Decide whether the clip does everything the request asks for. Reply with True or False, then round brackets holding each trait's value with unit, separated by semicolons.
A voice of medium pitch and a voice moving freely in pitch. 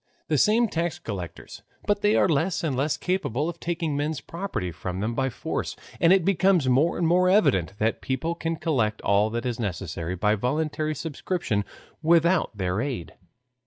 True (145 Hz; 8.0 semitones)